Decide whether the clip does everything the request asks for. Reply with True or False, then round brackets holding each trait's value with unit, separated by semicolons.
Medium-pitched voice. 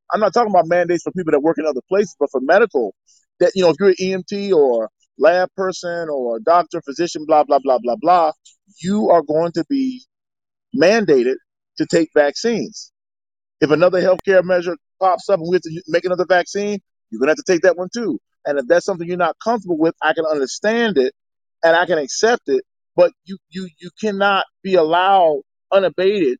True (180 Hz)